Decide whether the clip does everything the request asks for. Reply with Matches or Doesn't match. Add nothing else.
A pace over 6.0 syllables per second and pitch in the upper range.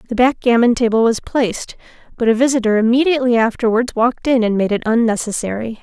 Matches